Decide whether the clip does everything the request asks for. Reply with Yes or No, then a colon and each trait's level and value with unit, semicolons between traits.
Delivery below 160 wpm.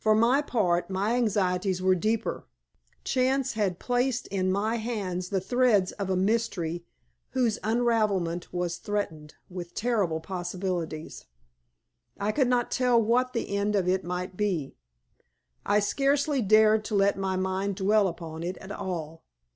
Yes: average, 145 wpm